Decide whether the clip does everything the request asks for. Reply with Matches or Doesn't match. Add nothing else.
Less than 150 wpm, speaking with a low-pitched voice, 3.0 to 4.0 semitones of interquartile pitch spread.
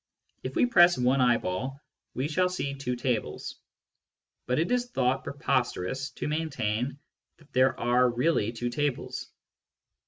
Matches